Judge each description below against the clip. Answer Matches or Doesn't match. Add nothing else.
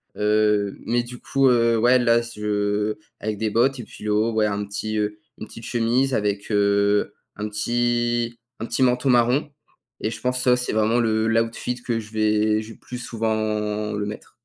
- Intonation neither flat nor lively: Doesn't match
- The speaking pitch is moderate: Doesn't match